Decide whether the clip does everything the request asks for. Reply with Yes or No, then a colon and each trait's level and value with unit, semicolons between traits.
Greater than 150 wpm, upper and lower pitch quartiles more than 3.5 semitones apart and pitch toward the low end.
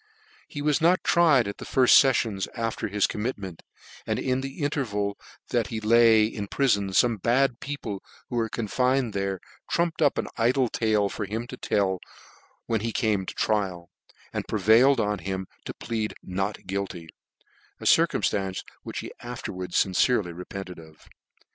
Yes: average, 160 wpm; average, 4.3 semitones; low, 110 Hz